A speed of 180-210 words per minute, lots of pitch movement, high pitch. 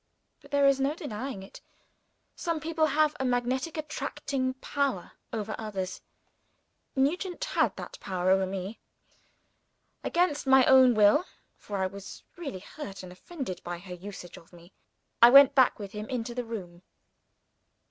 No: average, 150 wpm; wide, 6.6 semitones; high, 245 Hz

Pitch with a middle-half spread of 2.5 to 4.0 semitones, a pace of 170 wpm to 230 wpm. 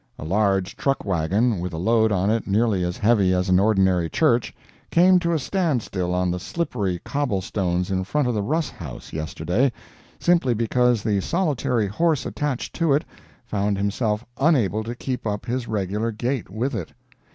No: wide, 5.4 semitones; average, 180 wpm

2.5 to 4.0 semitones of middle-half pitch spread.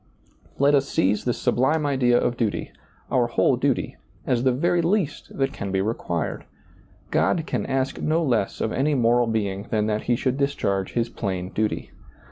No: average, 4.7 semitones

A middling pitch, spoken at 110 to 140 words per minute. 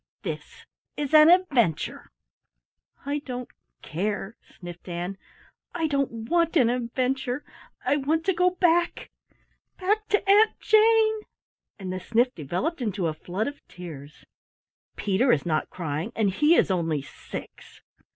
No: very high, 250 Hz; slow, 135 wpm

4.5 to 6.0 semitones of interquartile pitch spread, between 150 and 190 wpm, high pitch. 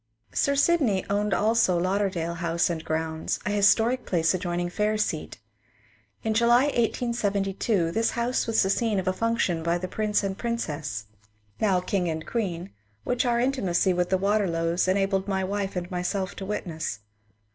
No: average, 4.1 semitones; average, 170 wpm; high, 195 Hz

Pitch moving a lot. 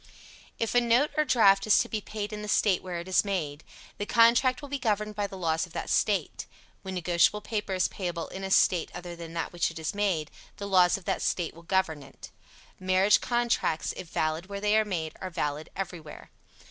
No: average, 3.7 semitones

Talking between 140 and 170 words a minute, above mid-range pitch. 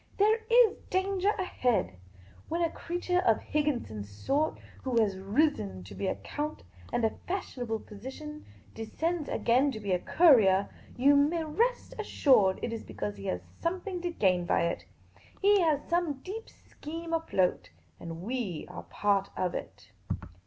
Yes: average, 160 wpm; very high, 275 Hz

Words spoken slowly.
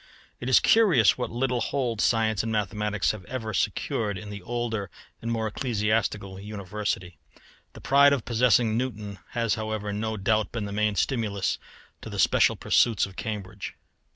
No: average, 160 wpm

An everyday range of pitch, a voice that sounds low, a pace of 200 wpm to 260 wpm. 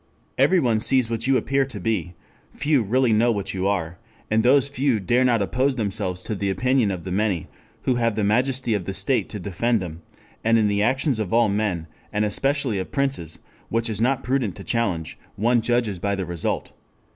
Yes: average, 4.3 semitones; low, 110 Hz; fast, 205 wpm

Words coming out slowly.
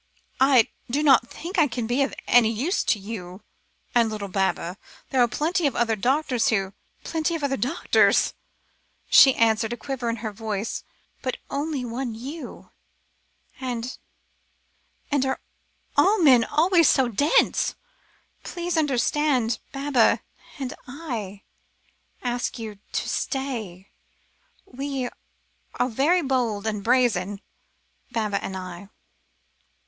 Yes: slow, 130 wpm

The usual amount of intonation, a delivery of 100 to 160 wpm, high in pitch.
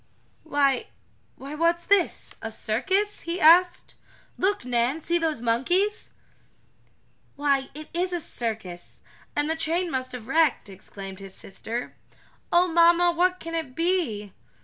No: wide, 6.3 semitones; average, 140 wpm; very high, 310 Hz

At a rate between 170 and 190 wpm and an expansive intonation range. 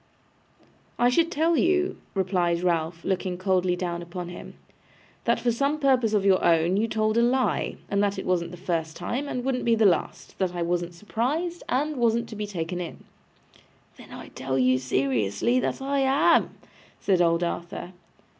Yes: average, 180 wpm; wide, 6.2 semitones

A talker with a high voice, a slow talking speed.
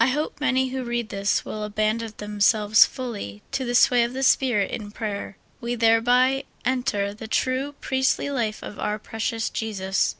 No: high, 230 Hz; average, 175 wpm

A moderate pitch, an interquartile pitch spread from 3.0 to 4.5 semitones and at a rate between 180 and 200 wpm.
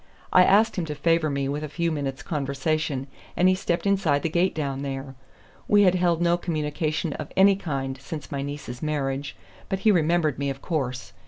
Yes: medium, 155 Hz; average, 3.8 semitones; average, 195 wpm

